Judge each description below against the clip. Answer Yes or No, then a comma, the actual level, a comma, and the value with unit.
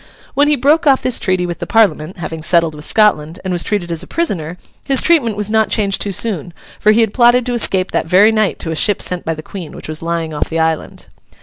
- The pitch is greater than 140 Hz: Yes, high, 190 Hz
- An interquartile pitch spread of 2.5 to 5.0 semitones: No, wide, 5.4 semitones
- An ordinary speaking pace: No, fast, 250 wpm